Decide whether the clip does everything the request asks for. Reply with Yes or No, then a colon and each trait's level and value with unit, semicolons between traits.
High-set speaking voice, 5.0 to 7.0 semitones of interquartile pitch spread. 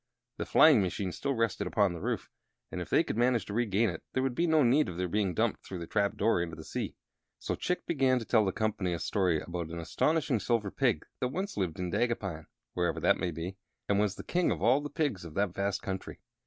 No: low, 100 Hz; wide, 5.5 semitones